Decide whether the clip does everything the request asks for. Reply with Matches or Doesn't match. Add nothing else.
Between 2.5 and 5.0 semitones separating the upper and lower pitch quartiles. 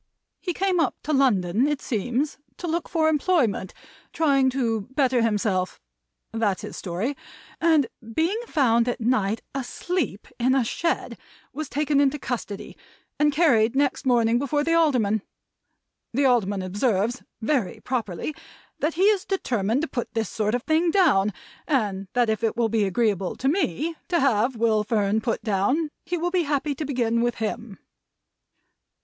Doesn't match